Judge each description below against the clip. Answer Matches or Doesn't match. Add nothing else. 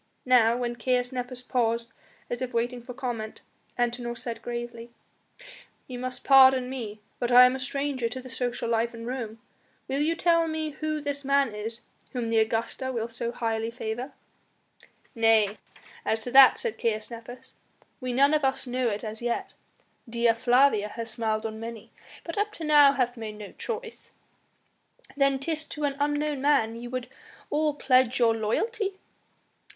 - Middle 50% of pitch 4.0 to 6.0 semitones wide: Doesn't match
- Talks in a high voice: Matches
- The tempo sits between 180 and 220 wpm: Doesn't match